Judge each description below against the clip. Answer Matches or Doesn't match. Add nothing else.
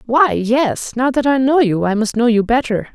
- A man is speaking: Doesn't match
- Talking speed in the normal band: Doesn't match